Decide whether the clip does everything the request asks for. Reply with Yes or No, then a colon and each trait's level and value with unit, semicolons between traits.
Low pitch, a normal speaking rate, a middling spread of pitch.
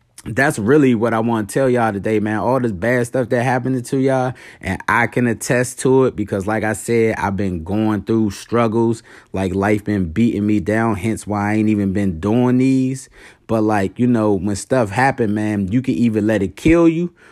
No: low, 115 Hz; fast, 215 wpm; average, 3.1 semitones